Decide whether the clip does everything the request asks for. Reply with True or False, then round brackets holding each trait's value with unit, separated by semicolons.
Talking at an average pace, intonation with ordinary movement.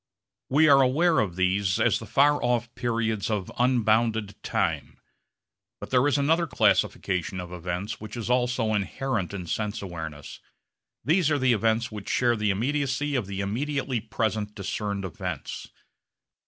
True (150 wpm; 4.6 semitones)